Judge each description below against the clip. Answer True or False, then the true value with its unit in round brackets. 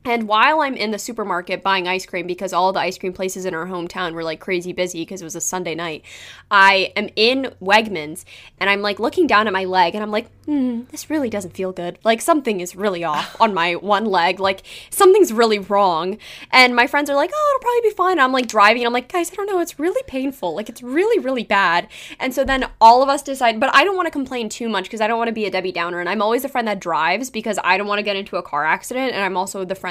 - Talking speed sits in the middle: False (275 wpm)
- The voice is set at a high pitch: True (210 Hz)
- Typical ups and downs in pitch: False (5.8 semitones)